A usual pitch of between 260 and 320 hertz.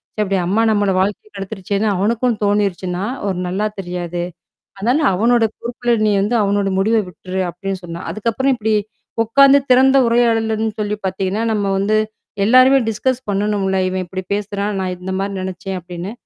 No: high, 205 Hz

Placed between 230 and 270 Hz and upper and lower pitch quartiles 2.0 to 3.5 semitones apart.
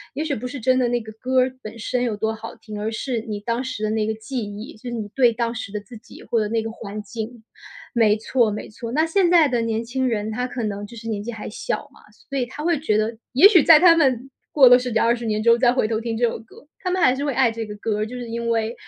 Yes: high, 235 Hz; average, 2.7 semitones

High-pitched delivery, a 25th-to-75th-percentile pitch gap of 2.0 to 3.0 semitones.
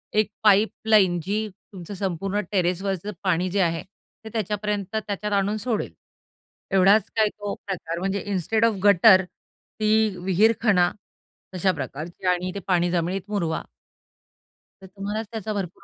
Yes: high, 195 Hz; narrow, 2.6 semitones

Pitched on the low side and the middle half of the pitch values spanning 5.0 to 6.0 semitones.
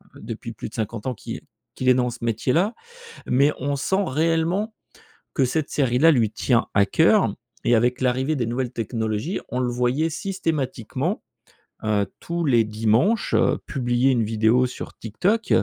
Yes: low, 125 Hz; wide, 5.6 semitones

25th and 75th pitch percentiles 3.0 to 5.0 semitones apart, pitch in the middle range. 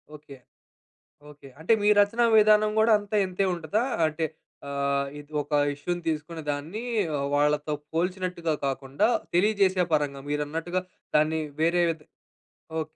Yes: average, 4.3 semitones; medium, 160 Hz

